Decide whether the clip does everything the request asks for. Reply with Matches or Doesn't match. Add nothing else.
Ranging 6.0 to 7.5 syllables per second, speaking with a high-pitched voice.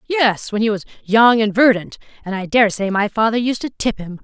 Doesn't match